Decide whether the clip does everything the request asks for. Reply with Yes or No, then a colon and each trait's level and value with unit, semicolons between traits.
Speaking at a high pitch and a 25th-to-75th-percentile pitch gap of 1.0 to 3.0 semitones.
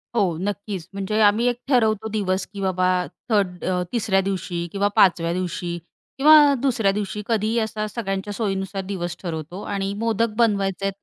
Yes: high, 200 Hz; average, 2.7 semitones